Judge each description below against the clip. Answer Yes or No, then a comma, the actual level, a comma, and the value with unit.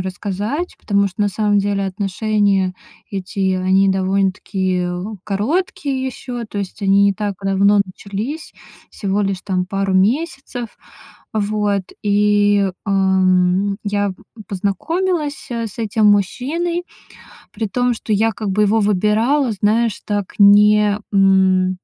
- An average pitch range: No, narrow, 2.3 semitones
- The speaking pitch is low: No, high, 205 Hz